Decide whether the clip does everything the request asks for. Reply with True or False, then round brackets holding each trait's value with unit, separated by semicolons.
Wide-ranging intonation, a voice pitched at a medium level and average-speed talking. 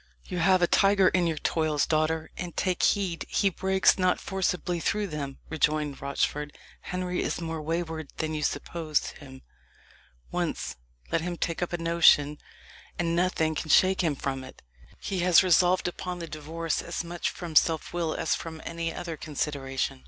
False (2.6 semitones; 165 Hz; 170 wpm)